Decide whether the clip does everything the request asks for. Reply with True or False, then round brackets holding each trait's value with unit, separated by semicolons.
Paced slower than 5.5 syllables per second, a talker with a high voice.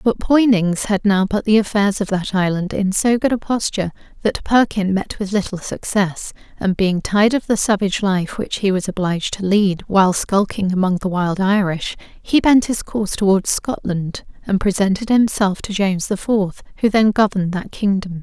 True (5.0 syllables/s; 200 Hz)